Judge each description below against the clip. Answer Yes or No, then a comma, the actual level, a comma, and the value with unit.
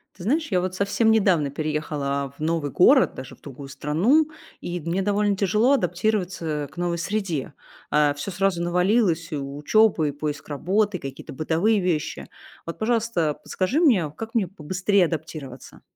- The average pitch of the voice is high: No, medium, 175 Hz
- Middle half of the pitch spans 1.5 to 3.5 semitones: No, wide, 5.4 semitones